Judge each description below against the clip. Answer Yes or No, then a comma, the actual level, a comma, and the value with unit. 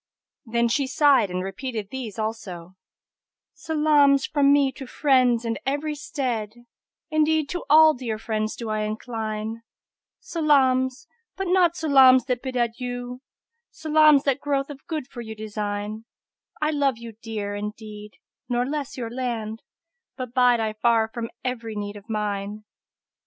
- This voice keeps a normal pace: Yes, average, 150 wpm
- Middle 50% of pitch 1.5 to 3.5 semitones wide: No, average, 4.5 semitones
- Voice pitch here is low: No, high, 245 Hz